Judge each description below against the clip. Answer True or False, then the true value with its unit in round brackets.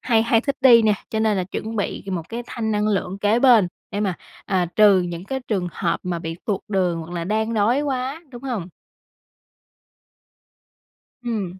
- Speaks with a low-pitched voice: False (210 Hz)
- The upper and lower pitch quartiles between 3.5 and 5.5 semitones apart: True (4.1 semitones)